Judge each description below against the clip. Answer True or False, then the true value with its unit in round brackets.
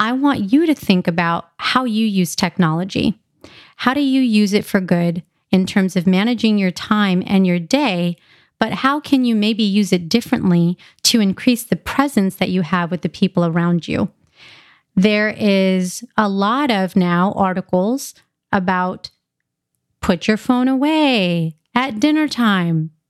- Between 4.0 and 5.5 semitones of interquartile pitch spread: True (4.7 semitones)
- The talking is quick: False (160 wpm)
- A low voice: False (200 Hz)